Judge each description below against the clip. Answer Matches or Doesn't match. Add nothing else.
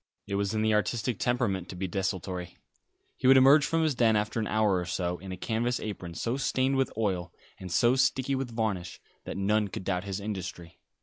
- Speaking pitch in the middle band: Doesn't match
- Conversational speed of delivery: Doesn't match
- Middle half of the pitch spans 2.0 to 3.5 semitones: Doesn't match